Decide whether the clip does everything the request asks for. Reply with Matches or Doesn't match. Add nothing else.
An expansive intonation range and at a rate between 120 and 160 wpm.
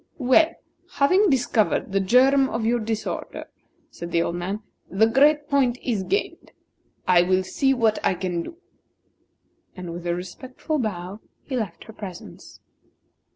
Matches